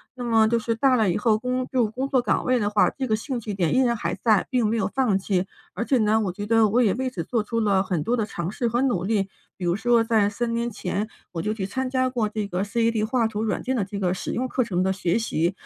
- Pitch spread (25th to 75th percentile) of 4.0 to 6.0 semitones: No, average, 3.3 semitones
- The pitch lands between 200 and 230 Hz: Yes, high, 220 Hz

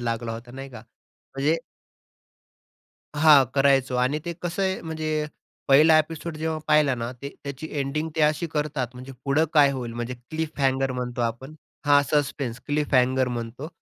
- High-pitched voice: No, medium, 140 Hz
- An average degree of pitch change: Yes, average, 3.4 semitones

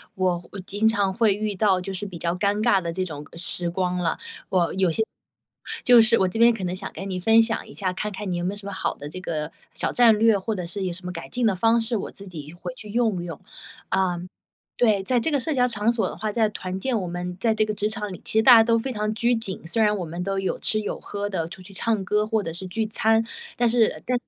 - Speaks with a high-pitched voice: Yes, high, 200 Hz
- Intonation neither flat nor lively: Yes, average, 3.5 semitones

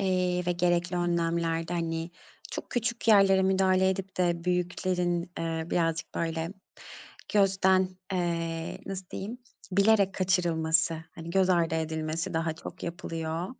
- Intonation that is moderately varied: No, narrow, 2.3 semitones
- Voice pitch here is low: No, medium, 175 Hz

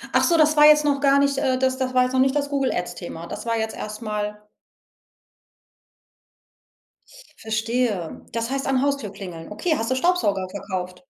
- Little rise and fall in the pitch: No, average, 5.0 semitones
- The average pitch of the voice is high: Yes, very high, 250 Hz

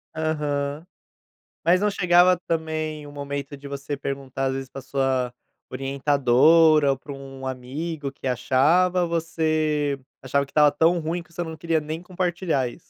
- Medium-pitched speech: Yes, medium, 145 Hz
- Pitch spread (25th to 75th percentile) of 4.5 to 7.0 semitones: No, average, 3.2 semitones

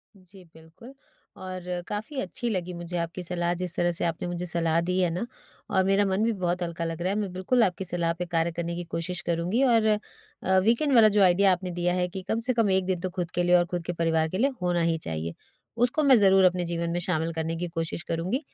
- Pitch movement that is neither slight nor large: No, narrow, 2.3 semitones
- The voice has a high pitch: No, medium, 180 Hz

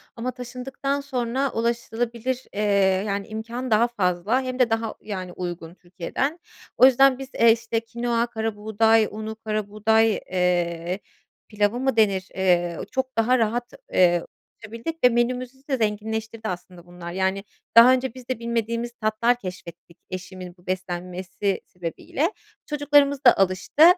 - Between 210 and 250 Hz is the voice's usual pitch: Yes, high, 225 Hz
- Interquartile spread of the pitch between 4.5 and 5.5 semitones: Yes, average, 4.8 semitones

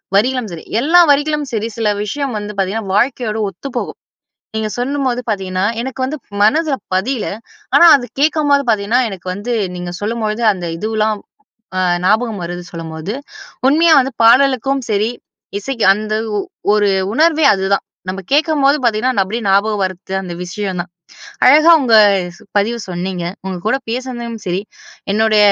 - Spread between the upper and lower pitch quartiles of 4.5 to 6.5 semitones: Yes, average, 5.1 semitones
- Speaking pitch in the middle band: No, high, 220 Hz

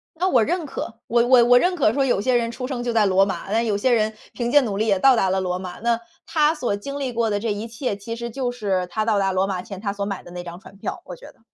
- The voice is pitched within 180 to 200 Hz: No, high, 225 Hz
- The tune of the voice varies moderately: Yes, average, 3.8 semitones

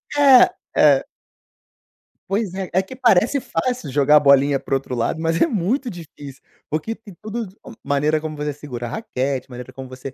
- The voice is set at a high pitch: No, medium, 155 Hz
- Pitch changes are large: Yes, wide, 7.7 semitones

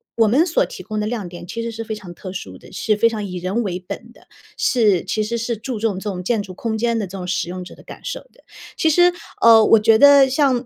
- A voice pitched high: Yes, high, 220 Hz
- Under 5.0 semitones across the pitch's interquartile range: Yes, average, 3.7 semitones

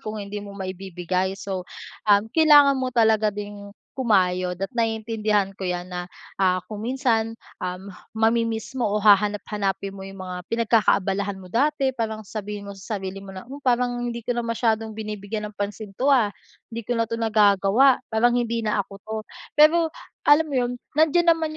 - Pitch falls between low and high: No, high, 215 Hz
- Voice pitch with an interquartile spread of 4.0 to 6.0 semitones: No, average, 3.3 semitones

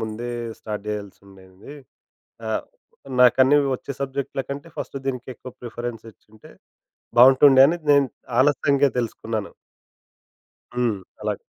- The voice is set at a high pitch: No, low, 125 Hz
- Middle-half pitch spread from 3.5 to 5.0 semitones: Yes, average, 4.2 semitones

